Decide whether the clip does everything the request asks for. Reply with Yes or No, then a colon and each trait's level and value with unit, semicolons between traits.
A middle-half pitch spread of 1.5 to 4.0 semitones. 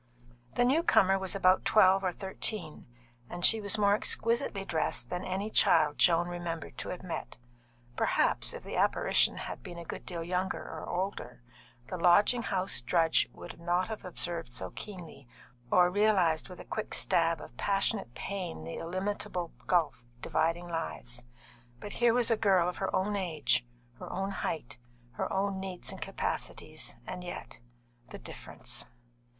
Yes: average, 3.1 semitones